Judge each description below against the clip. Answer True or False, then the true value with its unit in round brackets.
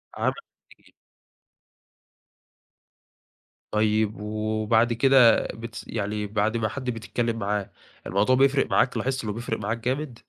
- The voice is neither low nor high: False (115 Hz)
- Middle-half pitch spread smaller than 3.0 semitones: True (2.5 semitones)